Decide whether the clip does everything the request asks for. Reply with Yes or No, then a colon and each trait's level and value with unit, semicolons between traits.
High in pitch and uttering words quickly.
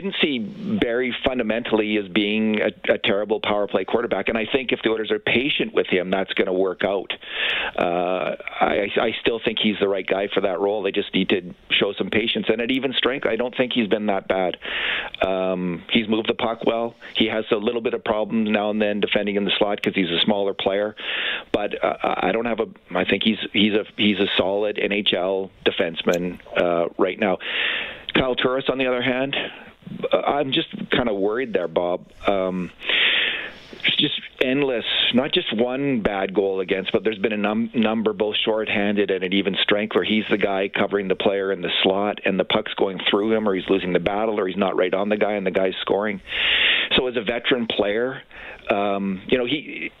No: low, 105 Hz; fast, 210 wpm